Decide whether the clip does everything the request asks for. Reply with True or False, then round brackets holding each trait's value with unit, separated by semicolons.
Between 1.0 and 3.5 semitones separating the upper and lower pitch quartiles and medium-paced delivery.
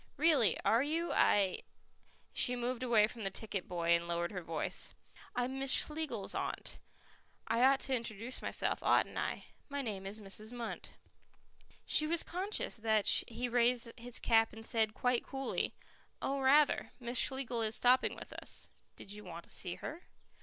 False (3.9 semitones; 175 wpm)